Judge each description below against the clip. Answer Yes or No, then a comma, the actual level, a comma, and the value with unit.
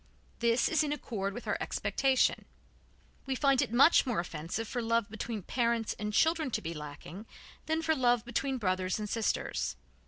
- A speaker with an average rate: Yes, average, 175 wpm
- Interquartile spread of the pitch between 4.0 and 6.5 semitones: Yes, average, 4.6 semitones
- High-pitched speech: Yes, high, 235 Hz